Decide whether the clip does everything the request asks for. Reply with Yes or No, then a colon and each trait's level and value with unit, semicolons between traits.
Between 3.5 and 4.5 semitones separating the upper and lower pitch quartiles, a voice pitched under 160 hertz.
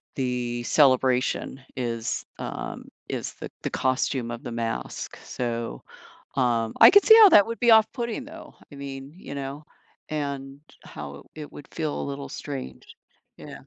Yes: average, 4.2 semitones; low, 135 Hz